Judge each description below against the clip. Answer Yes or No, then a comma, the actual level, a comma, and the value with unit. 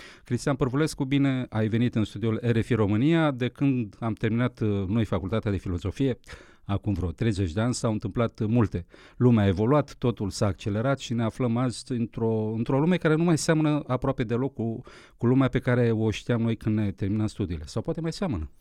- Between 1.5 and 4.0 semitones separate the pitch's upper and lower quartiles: Yes, average, 3.6 semitones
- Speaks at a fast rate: Yes, fast, 195 wpm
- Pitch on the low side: Yes, low, 115 Hz